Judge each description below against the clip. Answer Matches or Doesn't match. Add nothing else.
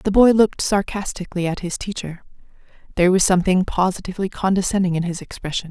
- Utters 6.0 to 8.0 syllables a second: Matches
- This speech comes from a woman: Matches